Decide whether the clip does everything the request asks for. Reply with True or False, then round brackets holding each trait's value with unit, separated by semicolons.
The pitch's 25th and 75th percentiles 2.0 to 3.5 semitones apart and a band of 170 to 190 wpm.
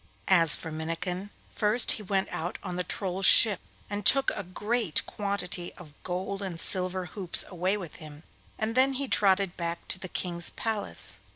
True (2.9 semitones; 175 wpm)